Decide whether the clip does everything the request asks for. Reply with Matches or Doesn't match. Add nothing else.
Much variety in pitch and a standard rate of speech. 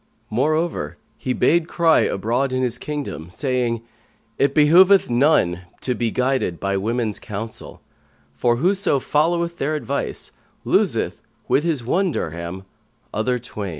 Doesn't match